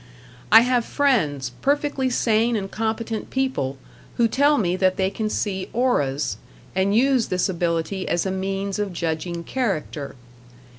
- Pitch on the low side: No, high, 200 Hz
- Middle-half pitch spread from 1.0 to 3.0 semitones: No, wide, 5.6 semitones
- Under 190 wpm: Yes, average, 145 wpm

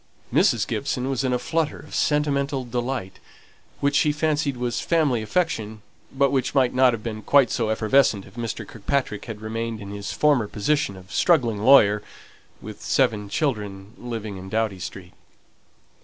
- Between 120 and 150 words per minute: No, average, 160 wpm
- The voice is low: Yes, low, 120 Hz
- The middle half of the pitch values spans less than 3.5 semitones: No, average, 4.8 semitones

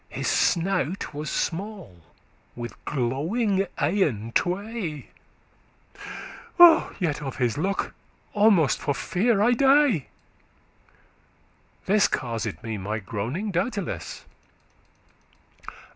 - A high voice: No, medium, 170 Hz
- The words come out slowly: Yes, slow, 90 wpm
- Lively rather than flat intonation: Yes, wide, 8.4 semitones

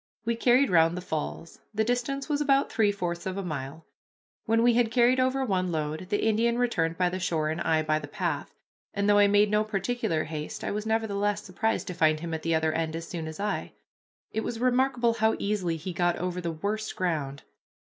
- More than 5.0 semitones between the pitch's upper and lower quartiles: Yes, wide, 5.6 semitones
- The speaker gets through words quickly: Yes, fast, 220 wpm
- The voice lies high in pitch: Yes, high, 195 Hz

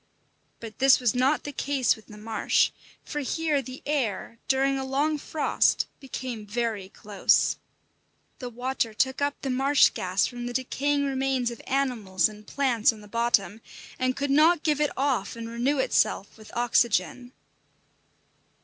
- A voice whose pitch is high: Yes, very high, 255 Hz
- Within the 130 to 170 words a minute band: Yes, average, 160 wpm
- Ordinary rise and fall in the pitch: Yes, average, 3.5 semitones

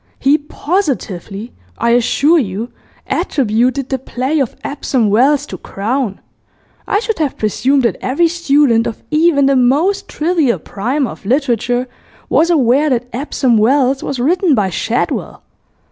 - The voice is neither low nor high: No, very high, 265 Hz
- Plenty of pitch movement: No, average, 4.1 semitones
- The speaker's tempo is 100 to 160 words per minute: Yes, average, 140 wpm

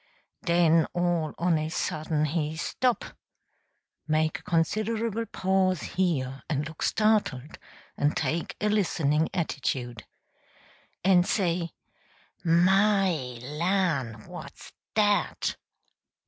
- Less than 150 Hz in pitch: No, medium, 170 Hz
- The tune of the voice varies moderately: Yes, average, 3.9 semitones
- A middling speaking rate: No, slow, 95 wpm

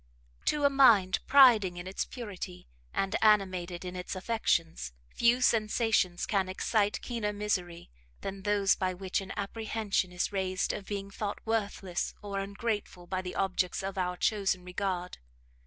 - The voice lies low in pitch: No, high, 195 Hz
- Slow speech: No, average, 150 wpm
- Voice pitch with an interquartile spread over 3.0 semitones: No, narrow, 2.6 semitones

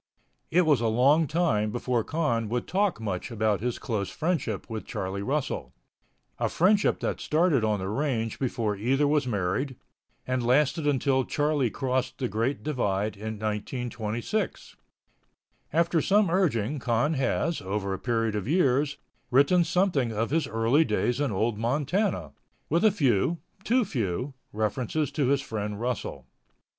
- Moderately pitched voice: No, low, 125 Hz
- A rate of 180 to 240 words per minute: No, average, 150 wpm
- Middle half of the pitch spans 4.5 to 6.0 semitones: Yes, wide, 5.5 semitones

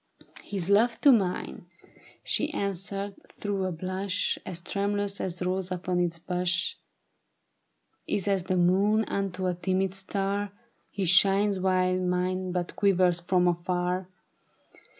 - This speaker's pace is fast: No, average, 140 wpm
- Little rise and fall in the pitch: Yes, narrow, 1.7 semitones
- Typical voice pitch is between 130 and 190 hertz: Yes, medium, 185 Hz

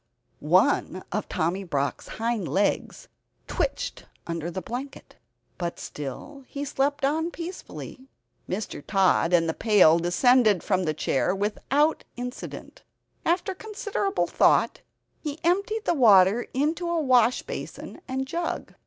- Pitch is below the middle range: No, high, 240 Hz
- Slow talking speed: Yes, slow, 125 wpm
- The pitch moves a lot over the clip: Yes, wide, 8.5 semitones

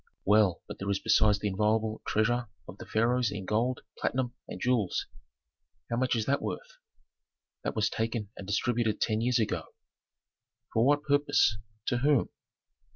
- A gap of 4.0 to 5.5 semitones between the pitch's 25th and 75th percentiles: No, average, 2.9 semitones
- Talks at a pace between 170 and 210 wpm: No, average, 160 wpm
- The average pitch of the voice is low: Yes, low, 115 Hz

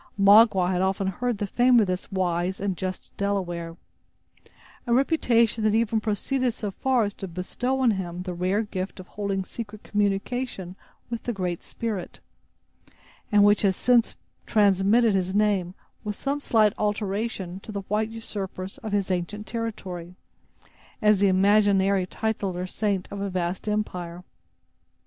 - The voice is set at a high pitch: Yes, high, 200 Hz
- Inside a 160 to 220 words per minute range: No, average, 150 wpm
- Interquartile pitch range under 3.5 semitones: Yes, average, 2.8 semitones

